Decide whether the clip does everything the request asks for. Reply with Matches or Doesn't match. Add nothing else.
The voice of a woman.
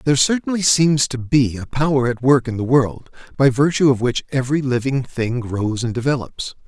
Doesn't match